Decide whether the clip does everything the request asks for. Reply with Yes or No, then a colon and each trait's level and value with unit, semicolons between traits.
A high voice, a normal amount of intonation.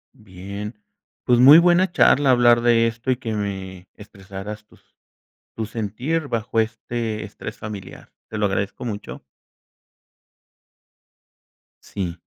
No: low, 110 Hz; average, 3.2 semitones